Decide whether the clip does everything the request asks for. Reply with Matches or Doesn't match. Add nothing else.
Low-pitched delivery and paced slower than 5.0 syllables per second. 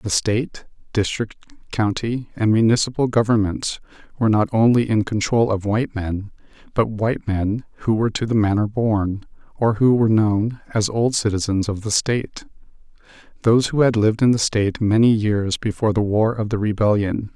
Doesn't match